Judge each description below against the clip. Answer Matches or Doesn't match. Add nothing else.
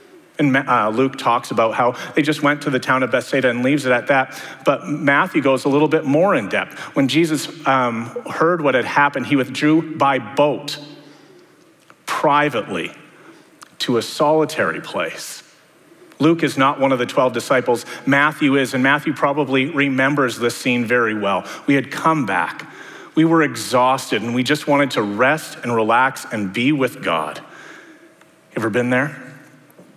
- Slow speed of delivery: Doesn't match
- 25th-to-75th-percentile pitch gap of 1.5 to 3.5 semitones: Matches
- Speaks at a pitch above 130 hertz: Matches